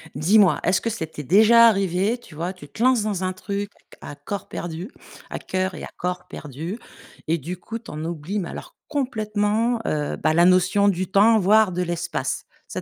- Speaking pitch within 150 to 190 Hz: Yes, medium, 185 Hz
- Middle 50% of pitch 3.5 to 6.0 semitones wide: Yes, average, 4.0 semitones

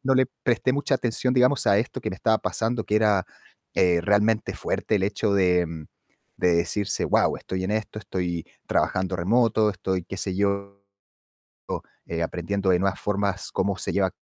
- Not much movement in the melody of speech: No, average, 3.0 semitones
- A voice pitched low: Yes, low, 100 Hz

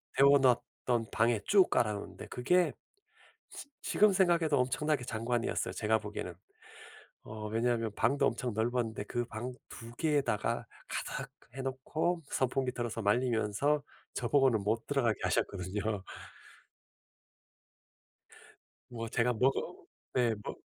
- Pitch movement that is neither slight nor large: Yes, average, 3.7 semitones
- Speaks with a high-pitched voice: No, low, 120 Hz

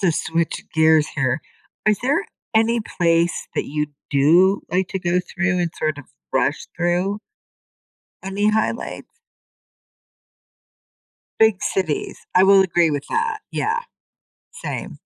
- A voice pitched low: No, medium, 180 Hz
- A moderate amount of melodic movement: Yes, average, 4.2 semitones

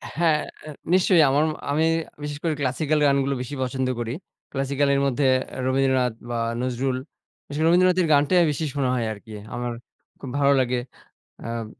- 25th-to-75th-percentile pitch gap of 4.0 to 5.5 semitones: No, average, 3.1 semitones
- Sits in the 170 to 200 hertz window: No, medium, 140 Hz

